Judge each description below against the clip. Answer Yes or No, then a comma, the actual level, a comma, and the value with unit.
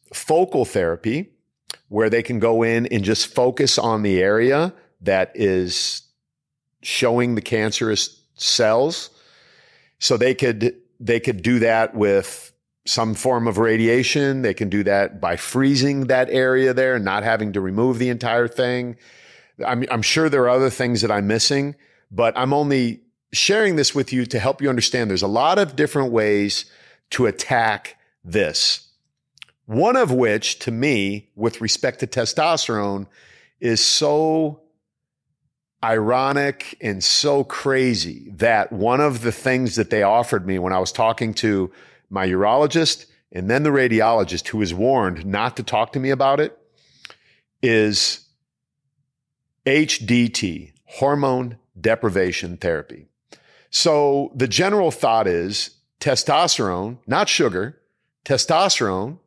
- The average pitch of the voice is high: No, low, 120 Hz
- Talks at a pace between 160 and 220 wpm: No, average, 140 wpm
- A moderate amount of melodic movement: Yes, average, 3.9 semitones